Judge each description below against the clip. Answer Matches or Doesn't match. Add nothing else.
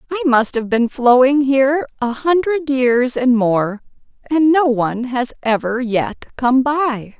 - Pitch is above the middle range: Matches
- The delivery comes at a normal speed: Matches